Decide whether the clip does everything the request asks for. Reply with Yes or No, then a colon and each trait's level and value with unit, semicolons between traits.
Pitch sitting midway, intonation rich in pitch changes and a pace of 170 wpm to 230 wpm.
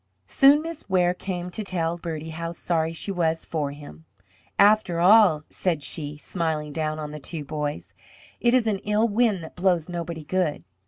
No: medium, 170 Hz; average, 3.8 semitones; average, 175 wpm